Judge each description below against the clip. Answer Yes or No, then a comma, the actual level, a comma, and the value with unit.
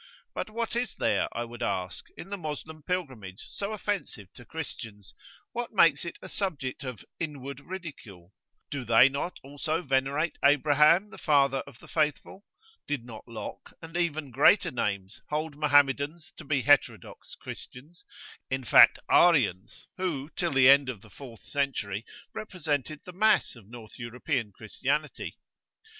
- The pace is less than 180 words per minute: Yes, average, 150 wpm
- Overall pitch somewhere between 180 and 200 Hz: No, medium, 140 Hz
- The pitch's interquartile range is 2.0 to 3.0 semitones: No, average, 5.1 semitones